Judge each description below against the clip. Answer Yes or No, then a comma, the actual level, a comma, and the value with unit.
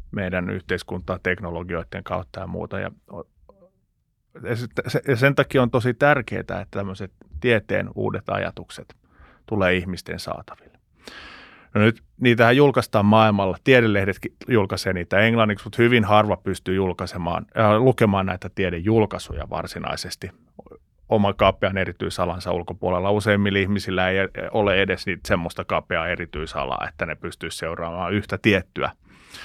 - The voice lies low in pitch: Yes, low, 100 Hz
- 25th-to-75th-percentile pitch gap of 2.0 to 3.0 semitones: No, average, 3.5 semitones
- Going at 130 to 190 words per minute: No, average, 115 wpm